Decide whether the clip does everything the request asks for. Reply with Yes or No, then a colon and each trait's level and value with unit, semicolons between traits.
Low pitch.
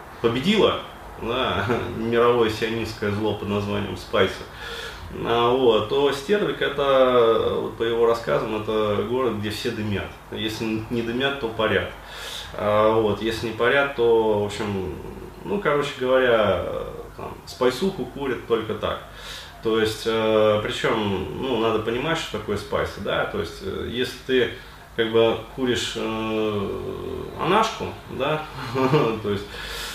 Yes: low, 115 Hz